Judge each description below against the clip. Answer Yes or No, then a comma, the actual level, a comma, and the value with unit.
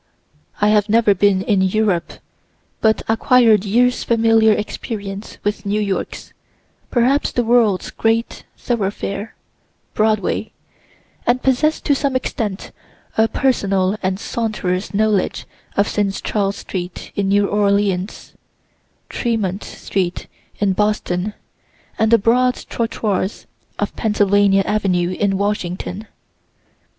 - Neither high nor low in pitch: No, high, 210 Hz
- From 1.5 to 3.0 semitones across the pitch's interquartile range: Yes, narrow, 2.4 semitones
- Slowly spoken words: Yes, slow, 110 wpm